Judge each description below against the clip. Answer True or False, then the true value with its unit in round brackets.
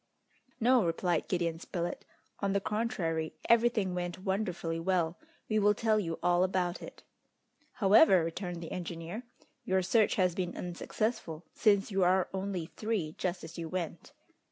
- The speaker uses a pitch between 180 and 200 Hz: True (185 Hz)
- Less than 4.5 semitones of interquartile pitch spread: True (3.3 semitones)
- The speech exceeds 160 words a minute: False (150 wpm)